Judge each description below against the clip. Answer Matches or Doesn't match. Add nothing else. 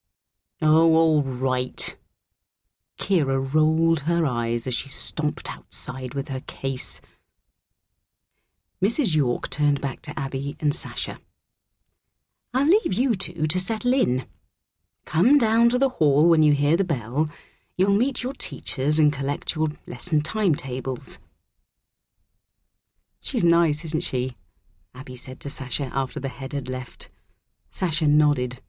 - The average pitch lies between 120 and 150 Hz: Matches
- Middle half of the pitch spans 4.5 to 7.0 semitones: Matches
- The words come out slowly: Matches